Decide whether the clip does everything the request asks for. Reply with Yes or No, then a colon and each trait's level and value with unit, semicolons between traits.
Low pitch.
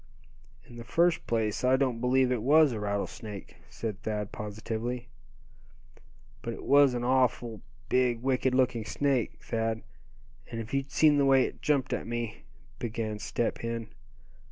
Yes: low, 120 Hz